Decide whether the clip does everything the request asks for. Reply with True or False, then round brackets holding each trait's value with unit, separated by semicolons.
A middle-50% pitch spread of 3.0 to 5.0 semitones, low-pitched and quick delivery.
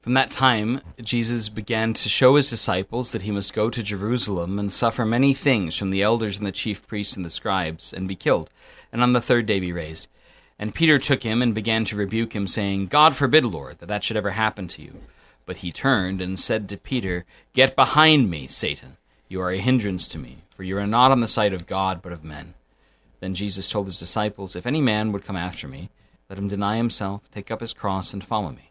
True (3.9 semitones; 105 Hz; 230 wpm)